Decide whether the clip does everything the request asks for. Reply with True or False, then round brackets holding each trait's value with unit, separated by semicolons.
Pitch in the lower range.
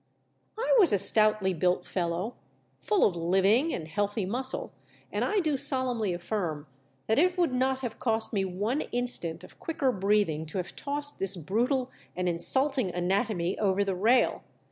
False (210 Hz)